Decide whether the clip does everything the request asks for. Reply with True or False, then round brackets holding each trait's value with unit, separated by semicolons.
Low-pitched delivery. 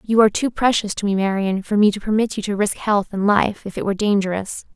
False (205 Hz)